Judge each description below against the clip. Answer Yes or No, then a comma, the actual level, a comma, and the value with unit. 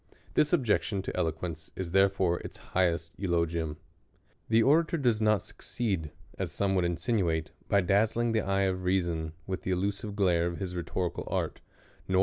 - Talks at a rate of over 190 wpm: No, average, 165 wpm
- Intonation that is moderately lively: Yes, average, 3.4 semitones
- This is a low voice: Yes, very low, 95 Hz